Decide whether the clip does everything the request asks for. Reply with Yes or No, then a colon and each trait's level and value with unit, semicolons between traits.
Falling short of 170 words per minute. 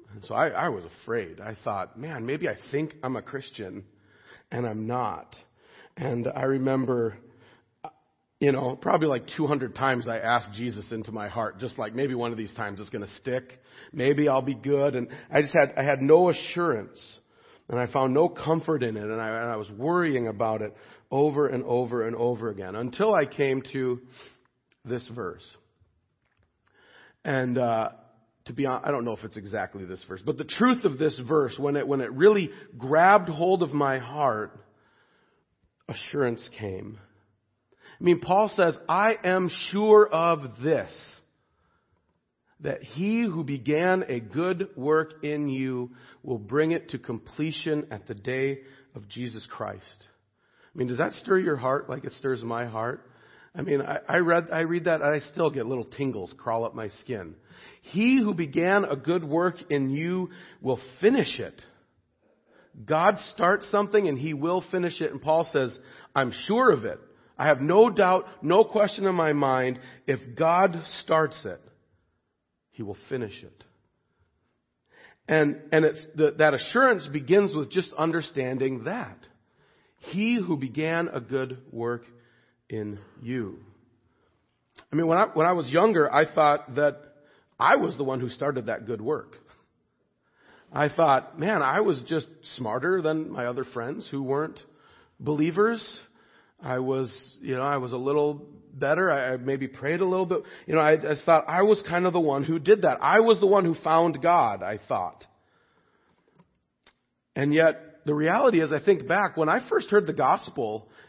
No: average, 175 wpm